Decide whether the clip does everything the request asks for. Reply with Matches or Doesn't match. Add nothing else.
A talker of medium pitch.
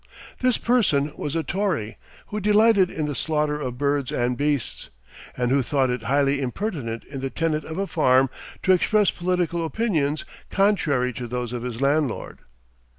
Matches